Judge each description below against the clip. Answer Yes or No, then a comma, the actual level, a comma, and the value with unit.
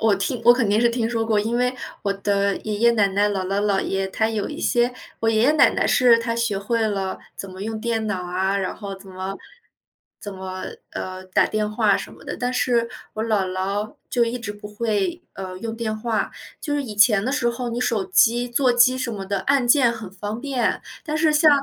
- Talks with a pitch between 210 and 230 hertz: Yes, high, 220 Hz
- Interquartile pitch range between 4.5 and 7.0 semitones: No, average, 3.2 semitones